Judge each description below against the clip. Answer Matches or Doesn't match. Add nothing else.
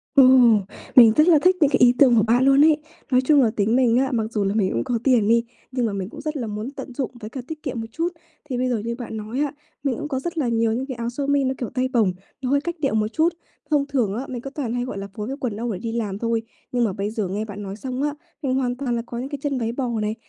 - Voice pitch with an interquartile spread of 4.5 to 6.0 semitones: Doesn't match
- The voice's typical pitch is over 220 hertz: Matches